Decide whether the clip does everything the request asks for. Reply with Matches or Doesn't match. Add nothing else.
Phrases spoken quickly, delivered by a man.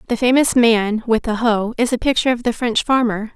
Doesn't match